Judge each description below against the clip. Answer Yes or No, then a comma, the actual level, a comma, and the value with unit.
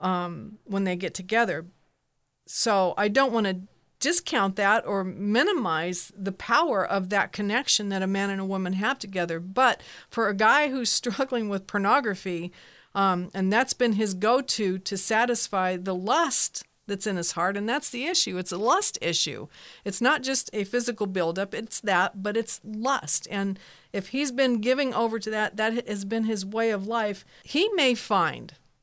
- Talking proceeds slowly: No, average, 180 wpm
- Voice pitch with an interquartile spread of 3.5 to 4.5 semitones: Yes, average, 3.9 semitones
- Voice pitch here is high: Yes, high, 205 Hz